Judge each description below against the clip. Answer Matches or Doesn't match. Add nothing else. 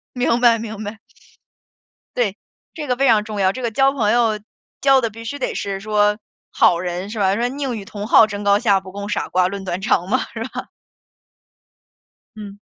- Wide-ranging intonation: Doesn't match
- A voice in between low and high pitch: Doesn't match